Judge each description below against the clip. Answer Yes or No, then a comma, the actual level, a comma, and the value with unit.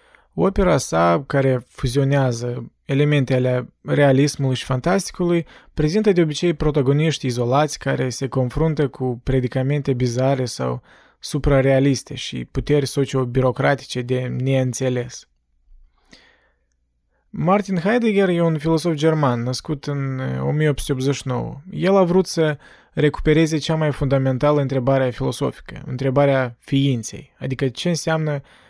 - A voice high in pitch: No, low, 135 Hz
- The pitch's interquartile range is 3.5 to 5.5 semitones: No, average, 3.1 semitones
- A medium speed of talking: No, slow, 105 wpm